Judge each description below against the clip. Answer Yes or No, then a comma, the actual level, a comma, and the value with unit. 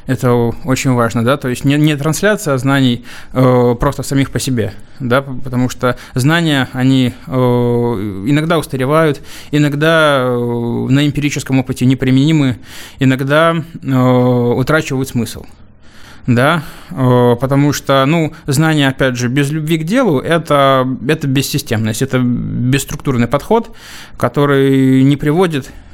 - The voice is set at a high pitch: No, low, 135 Hz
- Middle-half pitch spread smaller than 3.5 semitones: Yes, average, 2.8 semitones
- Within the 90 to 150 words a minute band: Yes, average, 125 wpm